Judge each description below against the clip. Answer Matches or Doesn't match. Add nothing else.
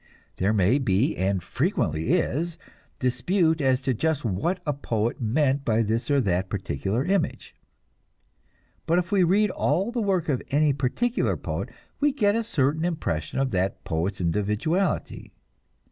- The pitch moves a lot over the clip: Matches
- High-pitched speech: Doesn't match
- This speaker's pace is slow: Doesn't match